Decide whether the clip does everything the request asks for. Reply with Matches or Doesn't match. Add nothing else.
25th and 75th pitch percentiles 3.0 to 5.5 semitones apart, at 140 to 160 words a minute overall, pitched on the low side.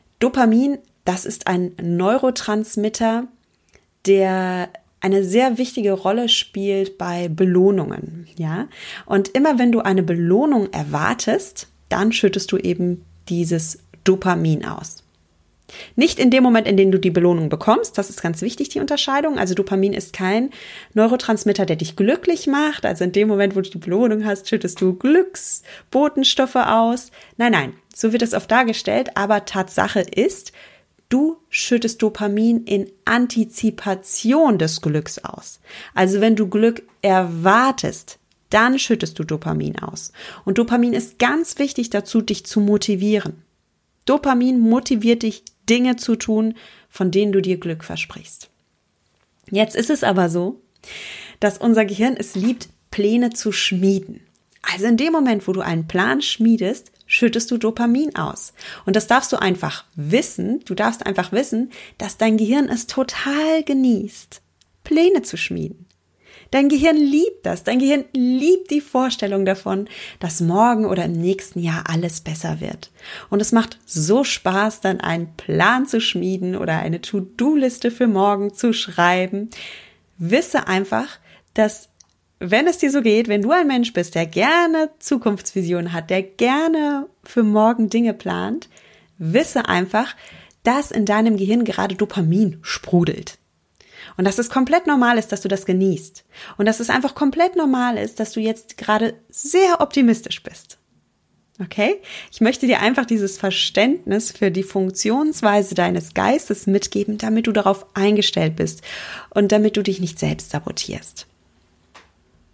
Doesn't match